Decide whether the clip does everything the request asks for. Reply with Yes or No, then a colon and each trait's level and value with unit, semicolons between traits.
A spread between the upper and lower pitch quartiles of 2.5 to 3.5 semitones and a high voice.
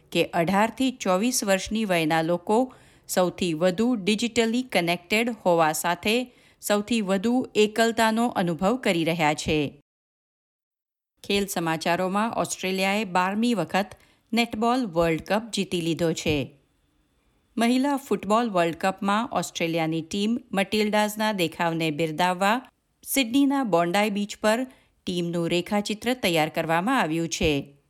No: average, 5.0 semitones; high, 200 Hz